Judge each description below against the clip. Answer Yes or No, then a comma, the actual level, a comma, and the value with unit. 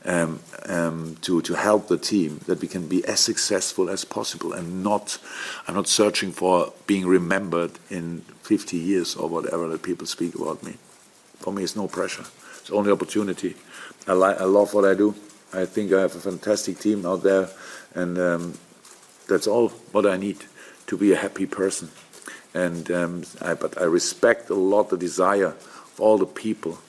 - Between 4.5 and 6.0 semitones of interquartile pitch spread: No, average, 2.8 semitones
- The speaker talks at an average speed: Yes, average, 185 wpm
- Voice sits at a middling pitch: No, very low, 95 Hz